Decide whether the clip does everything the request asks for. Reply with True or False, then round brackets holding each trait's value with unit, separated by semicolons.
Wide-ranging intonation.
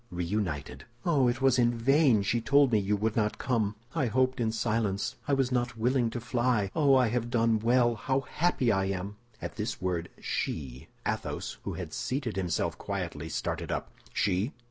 False (3.9 semitones)